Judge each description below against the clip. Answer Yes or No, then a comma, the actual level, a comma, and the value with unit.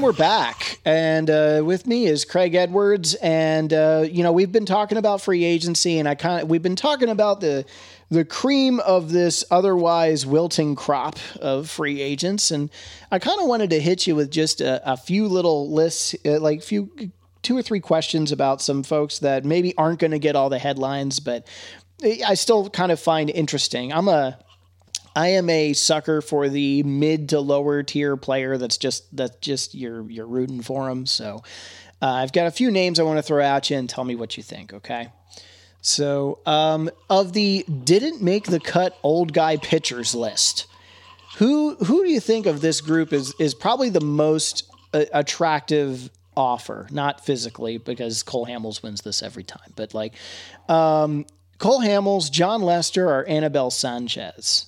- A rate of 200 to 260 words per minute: No, average, 185 wpm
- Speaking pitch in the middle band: Yes, medium, 155 Hz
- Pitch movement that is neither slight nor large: Yes, average, 4.6 semitones